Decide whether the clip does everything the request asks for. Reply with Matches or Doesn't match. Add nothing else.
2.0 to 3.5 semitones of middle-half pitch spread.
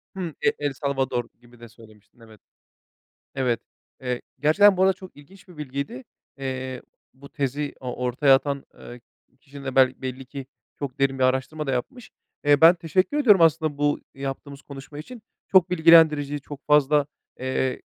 Matches